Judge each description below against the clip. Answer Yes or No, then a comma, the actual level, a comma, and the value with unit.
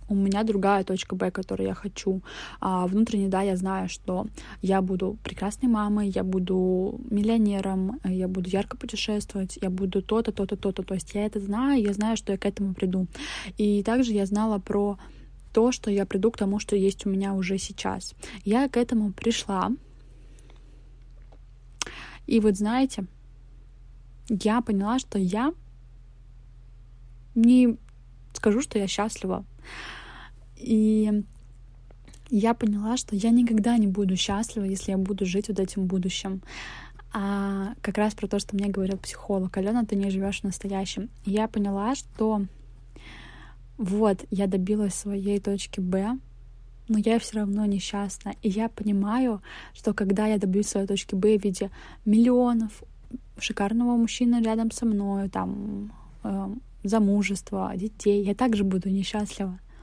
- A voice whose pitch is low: No, high, 200 Hz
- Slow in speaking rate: No, average, 145 wpm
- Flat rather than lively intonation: Yes, narrow, 2.1 semitones